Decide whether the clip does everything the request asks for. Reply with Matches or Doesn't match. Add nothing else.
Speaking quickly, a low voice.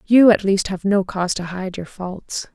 Doesn't match